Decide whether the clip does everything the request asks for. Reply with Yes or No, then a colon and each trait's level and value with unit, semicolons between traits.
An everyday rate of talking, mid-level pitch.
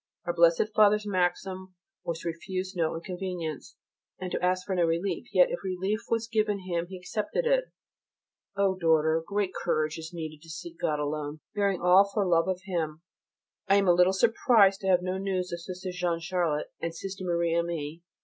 Yes: average, 190 wpm; medium, 180 Hz